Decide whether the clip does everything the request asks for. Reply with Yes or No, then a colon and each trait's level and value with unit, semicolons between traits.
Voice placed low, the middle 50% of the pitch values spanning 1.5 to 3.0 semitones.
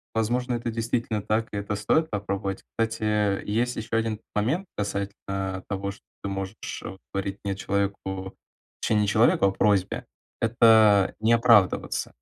Yes: low, 105 Hz; narrow, 2.4 semitones